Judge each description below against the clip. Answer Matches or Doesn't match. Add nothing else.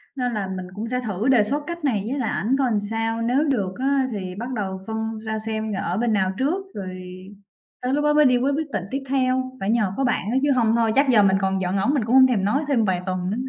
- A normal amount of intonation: Matches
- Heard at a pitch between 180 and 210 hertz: Doesn't match